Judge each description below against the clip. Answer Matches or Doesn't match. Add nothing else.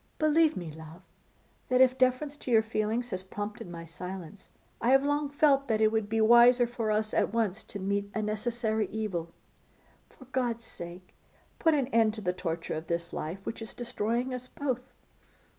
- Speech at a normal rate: Matches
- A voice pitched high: Matches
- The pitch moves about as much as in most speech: Matches